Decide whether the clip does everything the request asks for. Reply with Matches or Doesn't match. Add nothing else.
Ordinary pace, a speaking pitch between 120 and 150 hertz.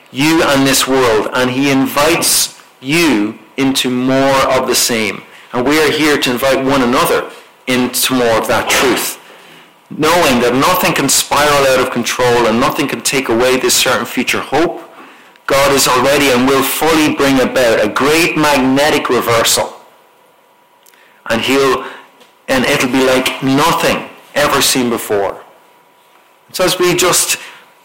Matches